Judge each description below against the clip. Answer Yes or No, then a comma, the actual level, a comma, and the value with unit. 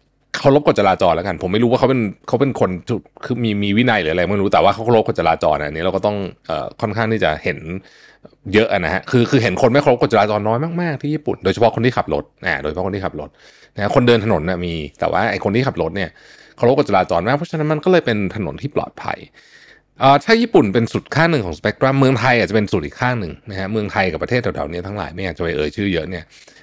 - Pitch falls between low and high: No, low, 110 Hz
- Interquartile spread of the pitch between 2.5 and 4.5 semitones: No, wide, 5.6 semitones